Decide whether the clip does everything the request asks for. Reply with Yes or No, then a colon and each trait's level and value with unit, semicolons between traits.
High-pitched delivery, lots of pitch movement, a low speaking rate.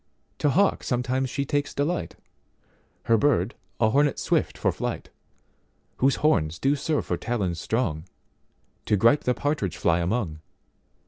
No: low, 125 Hz; wide, 7.4 semitones; slow, 125 wpm